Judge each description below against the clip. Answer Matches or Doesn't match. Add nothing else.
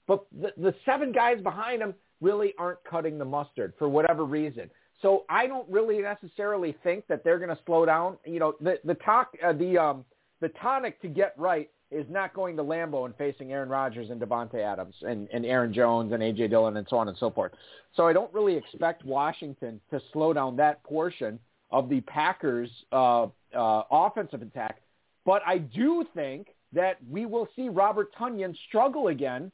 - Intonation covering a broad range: Matches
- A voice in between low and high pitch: Matches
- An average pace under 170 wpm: Doesn't match